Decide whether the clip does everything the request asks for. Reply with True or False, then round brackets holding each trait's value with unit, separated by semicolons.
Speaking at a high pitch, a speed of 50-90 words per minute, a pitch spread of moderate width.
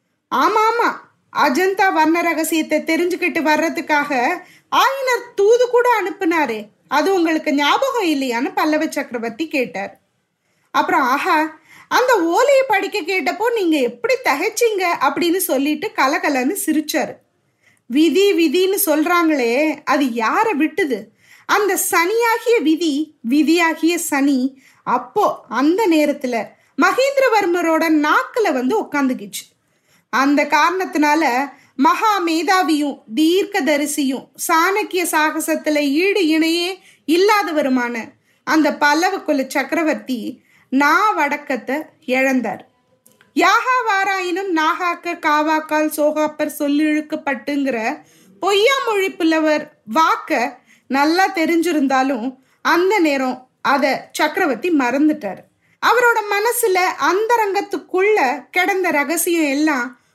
True (320 Hz; 85 wpm; 4.7 semitones)